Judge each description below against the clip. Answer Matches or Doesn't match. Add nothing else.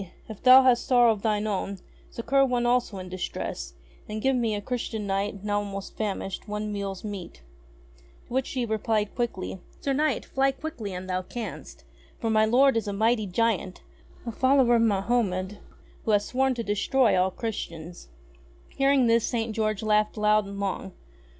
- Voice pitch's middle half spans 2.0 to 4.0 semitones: Matches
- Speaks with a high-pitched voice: Matches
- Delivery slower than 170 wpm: Doesn't match